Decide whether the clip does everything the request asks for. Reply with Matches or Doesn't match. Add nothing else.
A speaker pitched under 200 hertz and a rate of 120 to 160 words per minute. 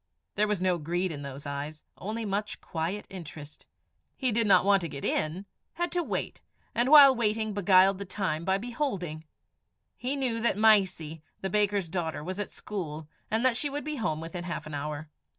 Doesn't match